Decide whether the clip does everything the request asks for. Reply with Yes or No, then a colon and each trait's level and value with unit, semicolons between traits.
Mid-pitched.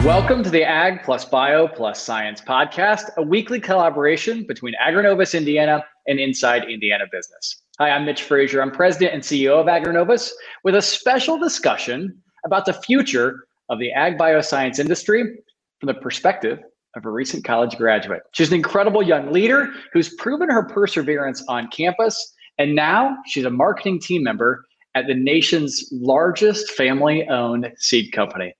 Yes: medium, 165 Hz